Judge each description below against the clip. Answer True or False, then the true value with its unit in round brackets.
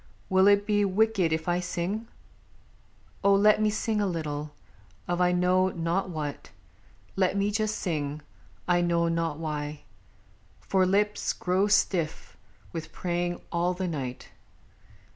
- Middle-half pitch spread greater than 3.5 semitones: False (3.2 semitones)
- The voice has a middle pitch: True (180 Hz)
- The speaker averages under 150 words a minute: True (140 wpm)